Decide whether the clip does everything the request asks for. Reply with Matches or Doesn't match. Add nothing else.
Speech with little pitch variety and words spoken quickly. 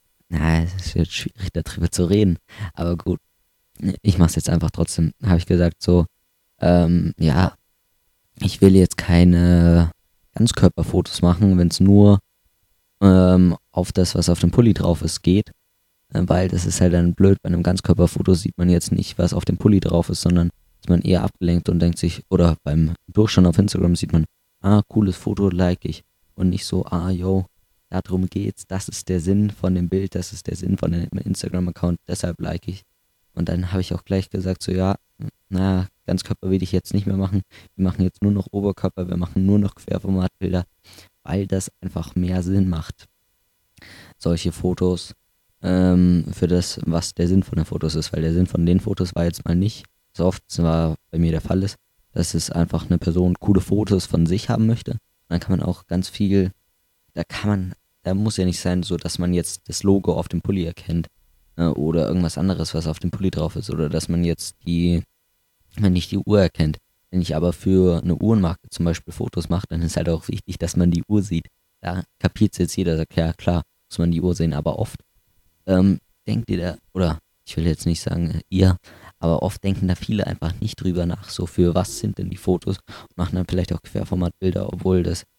Matches